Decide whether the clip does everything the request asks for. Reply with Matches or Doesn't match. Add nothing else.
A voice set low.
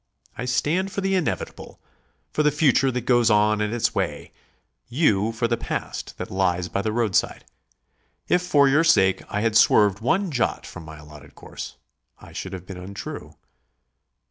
Matches